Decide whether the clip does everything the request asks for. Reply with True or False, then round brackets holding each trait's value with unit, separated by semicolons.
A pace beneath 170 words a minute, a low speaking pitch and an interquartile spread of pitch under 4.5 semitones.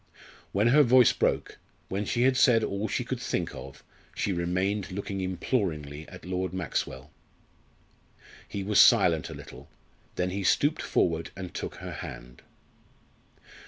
True (145 wpm; 95 Hz; 3.2 semitones)